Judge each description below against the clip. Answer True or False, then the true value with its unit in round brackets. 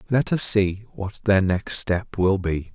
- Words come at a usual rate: True (195 wpm)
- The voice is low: True (100 Hz)